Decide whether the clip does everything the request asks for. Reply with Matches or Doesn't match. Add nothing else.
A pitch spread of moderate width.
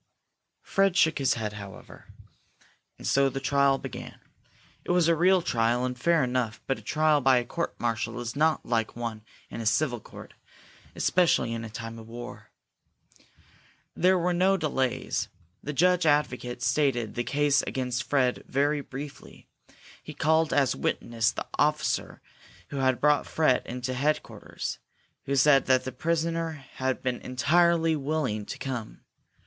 Matches